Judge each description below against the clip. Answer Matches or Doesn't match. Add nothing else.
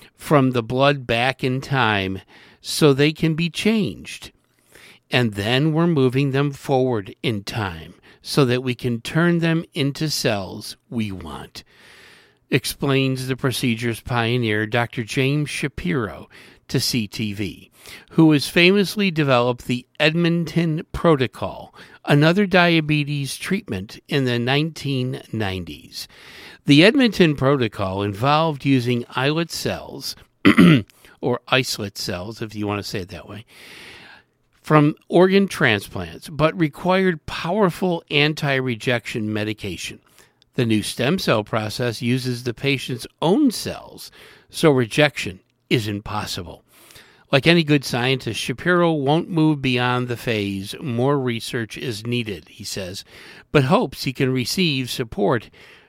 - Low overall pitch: Matches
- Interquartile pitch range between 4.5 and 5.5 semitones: Matches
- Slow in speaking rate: Matches